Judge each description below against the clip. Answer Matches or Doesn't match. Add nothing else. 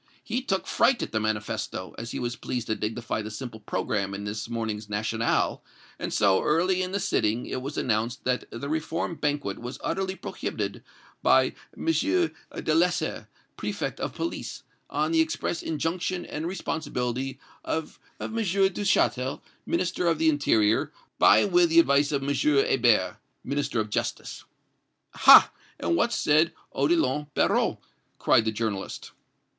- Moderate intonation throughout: Doesn't match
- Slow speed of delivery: Doesn't match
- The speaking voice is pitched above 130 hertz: Matches